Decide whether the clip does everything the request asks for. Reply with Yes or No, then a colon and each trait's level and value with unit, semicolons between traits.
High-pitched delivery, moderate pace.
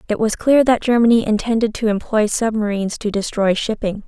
Yes: high, 220 Hz; average, 175 wpm